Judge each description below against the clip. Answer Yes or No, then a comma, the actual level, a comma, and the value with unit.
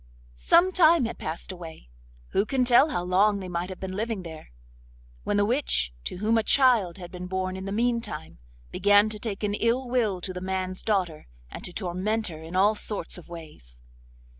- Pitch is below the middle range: No, high, 190 Hz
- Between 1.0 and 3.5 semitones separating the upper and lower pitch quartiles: No, average, 4.5 semitones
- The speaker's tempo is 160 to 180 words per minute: No, average, 190 wpm